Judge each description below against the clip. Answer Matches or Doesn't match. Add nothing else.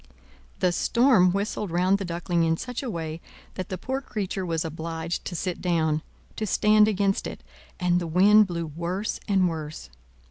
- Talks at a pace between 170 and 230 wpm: Matches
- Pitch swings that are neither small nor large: Matches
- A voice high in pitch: Doesn't match